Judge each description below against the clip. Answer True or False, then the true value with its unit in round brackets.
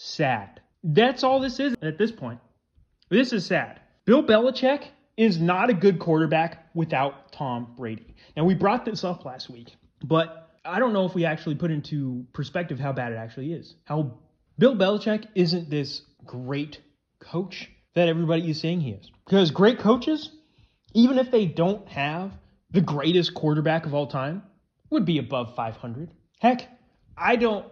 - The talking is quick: False (165 wpm)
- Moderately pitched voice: True (165 Hz)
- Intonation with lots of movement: True (6.6 semitones)